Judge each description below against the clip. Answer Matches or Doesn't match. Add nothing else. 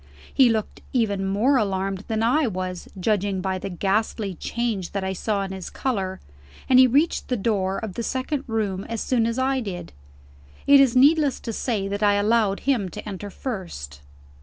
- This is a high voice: Matches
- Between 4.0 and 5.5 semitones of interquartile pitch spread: Matches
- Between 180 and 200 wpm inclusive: Matches